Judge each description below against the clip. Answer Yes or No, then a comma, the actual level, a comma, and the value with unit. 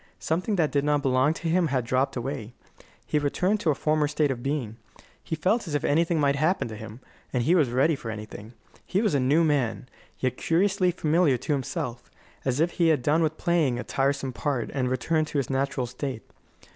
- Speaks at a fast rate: Yes, fast, 215 wpm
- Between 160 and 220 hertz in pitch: No, medium, 145 Hz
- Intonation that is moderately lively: Yes, average, 4.1 semitones